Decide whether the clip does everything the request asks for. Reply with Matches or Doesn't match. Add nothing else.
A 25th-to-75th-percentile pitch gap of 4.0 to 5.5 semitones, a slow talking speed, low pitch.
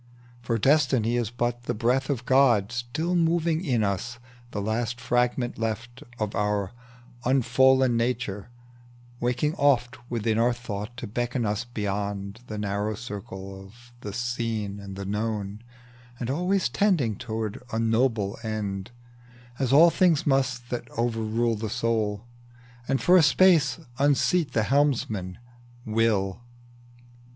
Doesn't match